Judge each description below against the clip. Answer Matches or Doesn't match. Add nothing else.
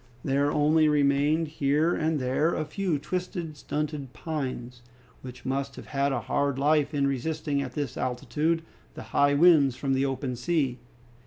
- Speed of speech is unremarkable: Matches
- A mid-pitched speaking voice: Matches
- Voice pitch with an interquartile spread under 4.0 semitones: Matches